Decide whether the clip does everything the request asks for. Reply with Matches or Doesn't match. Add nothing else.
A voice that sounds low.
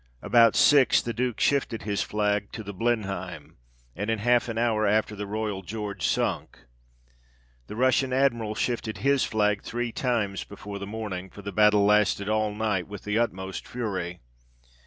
Matches